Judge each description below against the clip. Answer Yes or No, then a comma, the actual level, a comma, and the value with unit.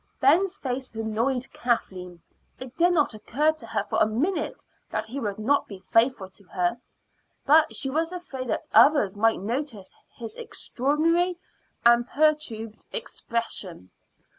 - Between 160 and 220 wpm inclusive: No, average, 140 wpm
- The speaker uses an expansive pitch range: Yes, wide, 5.7 semitones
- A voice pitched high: Yes, high, 245 Hz